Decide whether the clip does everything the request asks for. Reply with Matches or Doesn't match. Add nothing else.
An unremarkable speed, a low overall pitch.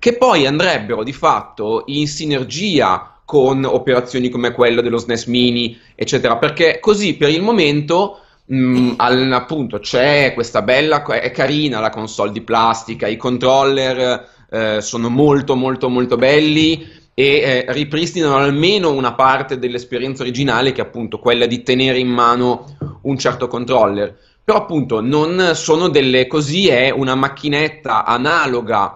Matches